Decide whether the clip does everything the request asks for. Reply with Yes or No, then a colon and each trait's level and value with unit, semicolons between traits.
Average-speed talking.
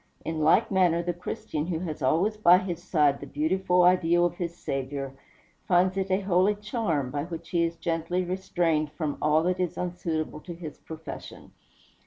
Yes: average, 180 wpm